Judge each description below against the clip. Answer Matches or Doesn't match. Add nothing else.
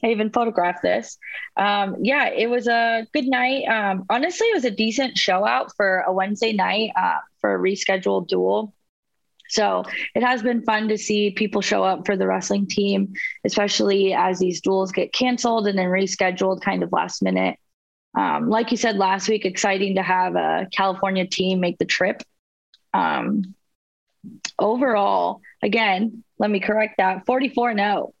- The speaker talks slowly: Doesn't match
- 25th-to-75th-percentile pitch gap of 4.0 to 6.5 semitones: Doesn't match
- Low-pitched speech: Doesn't match